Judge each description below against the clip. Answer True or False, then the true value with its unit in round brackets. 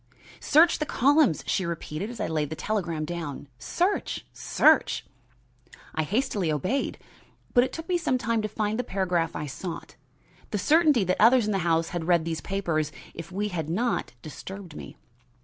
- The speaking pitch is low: False (190 Hz)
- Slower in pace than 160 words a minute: False (175 wpm)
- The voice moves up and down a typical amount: False (6.5 semitones)